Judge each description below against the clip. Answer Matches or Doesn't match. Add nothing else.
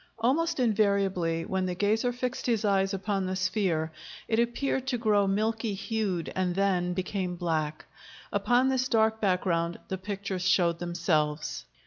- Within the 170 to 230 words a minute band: Doesn't match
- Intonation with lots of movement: Doesn't match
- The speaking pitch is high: Matches